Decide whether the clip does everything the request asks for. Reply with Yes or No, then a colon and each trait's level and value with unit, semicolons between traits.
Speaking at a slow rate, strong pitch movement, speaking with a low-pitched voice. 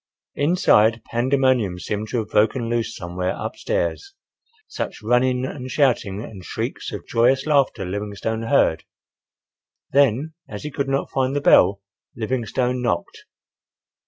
No: slow, 130 wpm; average, 4.3 semitones; low, 120 Hz